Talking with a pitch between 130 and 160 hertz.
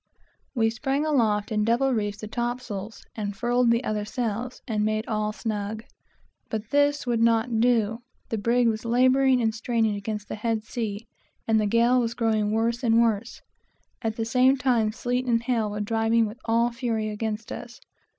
No: high, 225 Hz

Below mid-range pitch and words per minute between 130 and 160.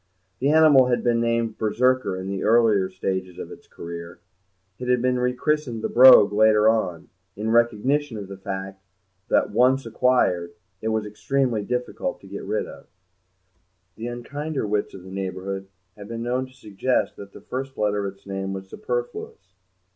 No: low, 110 Hz; average, 170 wpm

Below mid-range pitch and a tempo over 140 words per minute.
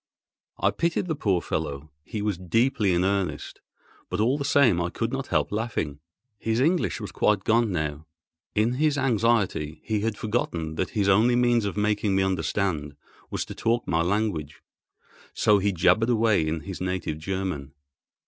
Yes: low, 100 Hz; average, 170 wpm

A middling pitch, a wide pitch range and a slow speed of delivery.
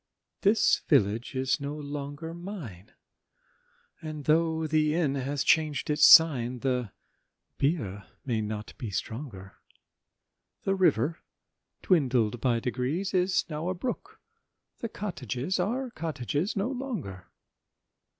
Yes: medium, 150 Hz; wide, 6.0 semitones; slow, 110 wpm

